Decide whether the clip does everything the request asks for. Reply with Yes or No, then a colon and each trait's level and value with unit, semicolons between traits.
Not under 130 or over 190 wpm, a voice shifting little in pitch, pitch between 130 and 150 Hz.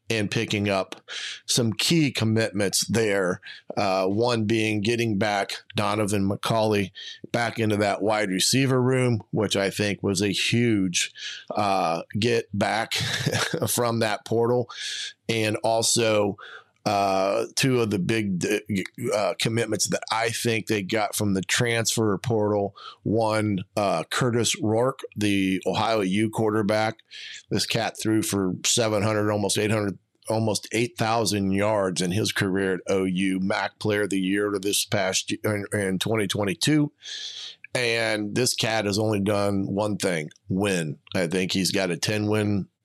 No: average, 140 wpm; narrow, 2.2 semitones; low, 105 Hz